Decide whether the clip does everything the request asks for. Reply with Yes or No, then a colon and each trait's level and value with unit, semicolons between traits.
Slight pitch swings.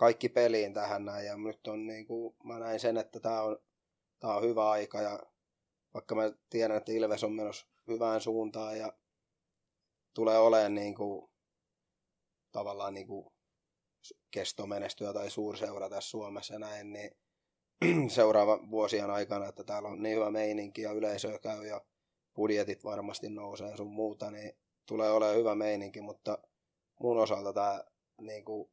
Yes: narrow, 1.0 semitones